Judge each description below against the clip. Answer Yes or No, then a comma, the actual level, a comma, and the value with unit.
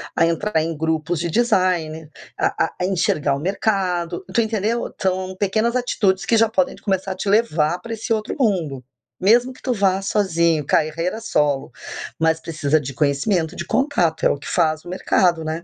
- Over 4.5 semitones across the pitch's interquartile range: Yes, average, 5.0 semitones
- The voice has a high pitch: No, medium, 180 Hz